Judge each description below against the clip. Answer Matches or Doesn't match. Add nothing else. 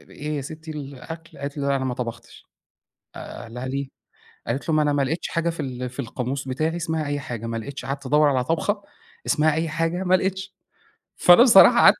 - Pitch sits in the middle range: Matches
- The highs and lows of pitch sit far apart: Doesn't match